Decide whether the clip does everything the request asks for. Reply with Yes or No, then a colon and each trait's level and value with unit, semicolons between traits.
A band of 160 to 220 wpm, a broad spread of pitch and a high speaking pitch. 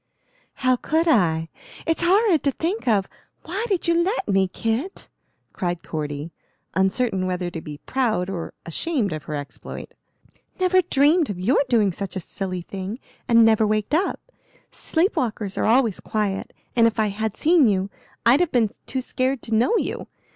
Yes: average, 170 wpm; wide, 8.0 semitones; high, 225 Hz